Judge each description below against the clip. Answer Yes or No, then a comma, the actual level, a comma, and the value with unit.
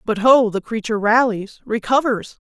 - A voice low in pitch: No, high, 225 Hz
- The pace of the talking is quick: No, slow, 120 wpm